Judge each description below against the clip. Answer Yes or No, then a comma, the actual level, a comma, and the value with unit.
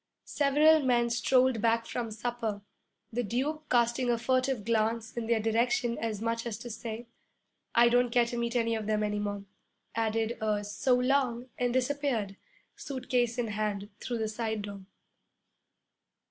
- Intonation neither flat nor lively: No, narrow, 2.1 semitones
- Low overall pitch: No, high, 235 Hz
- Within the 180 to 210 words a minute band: No, average, 160 wpm